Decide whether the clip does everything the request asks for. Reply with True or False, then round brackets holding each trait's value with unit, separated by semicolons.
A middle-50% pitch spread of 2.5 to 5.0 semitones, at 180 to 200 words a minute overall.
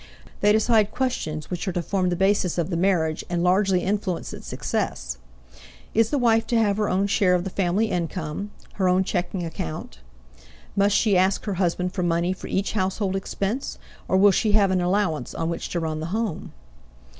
True (2.8 semitones; 195 wpm)